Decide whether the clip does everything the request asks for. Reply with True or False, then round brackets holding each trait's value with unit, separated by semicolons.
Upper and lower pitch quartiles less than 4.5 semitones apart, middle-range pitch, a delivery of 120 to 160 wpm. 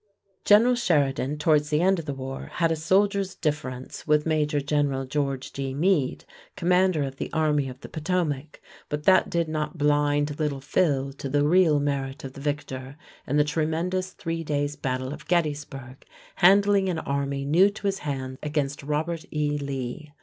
False (3.1 semitones; 150 Hz; 170 wpm)